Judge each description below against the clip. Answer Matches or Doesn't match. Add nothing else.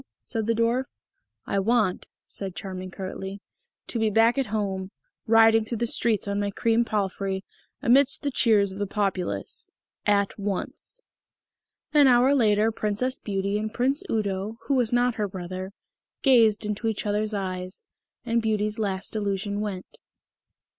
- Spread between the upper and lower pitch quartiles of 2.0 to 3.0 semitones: Matches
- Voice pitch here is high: Matches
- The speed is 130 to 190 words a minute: Matches